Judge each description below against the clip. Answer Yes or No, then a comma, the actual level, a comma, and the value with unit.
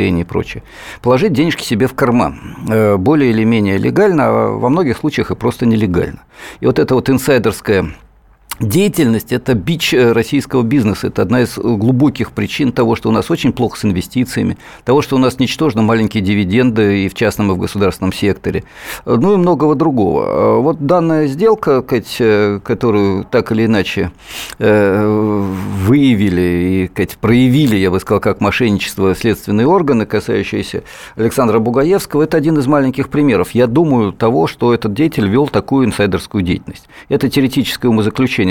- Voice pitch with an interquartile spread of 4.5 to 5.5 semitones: Yes, average, 4.9 semitones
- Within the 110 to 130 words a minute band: No, average, 150 wpm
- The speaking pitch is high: No, low, 115 Hz